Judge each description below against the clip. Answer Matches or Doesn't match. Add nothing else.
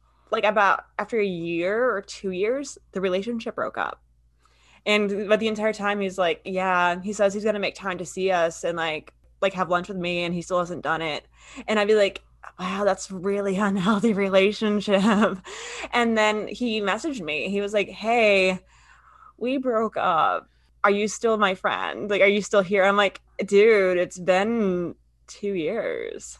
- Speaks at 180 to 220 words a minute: Matches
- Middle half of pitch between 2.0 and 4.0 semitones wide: Matches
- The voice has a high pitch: Matches